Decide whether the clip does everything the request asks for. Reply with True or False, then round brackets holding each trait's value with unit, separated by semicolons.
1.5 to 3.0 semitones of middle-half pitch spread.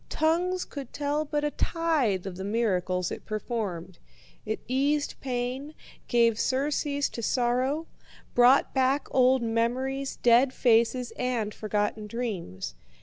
False (4.3 semitones)